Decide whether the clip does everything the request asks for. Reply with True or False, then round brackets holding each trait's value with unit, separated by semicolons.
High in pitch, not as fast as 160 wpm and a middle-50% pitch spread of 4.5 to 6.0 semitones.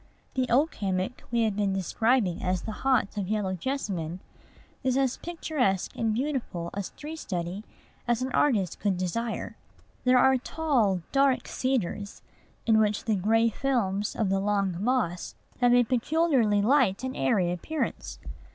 True (220 Hz; 150 wpm; 5.1 semitones)